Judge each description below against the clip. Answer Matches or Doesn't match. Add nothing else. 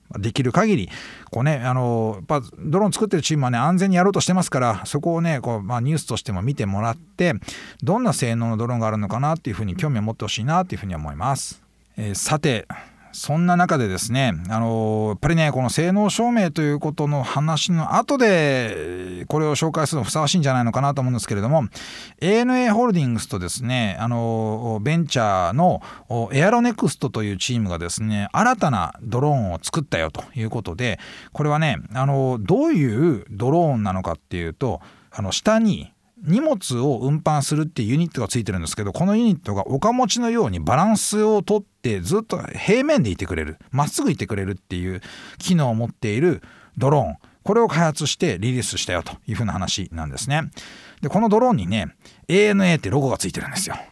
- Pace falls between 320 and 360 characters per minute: Doesn't match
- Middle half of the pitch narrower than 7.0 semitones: Doesn't match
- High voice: Doesn't match